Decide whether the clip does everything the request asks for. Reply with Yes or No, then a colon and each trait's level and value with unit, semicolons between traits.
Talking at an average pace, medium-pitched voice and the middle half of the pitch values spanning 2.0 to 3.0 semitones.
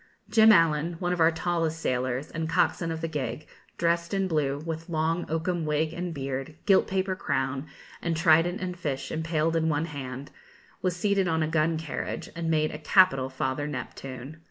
Yes: average, 180 wpm; medium, 160 Hz; narrow, 2.6 semitones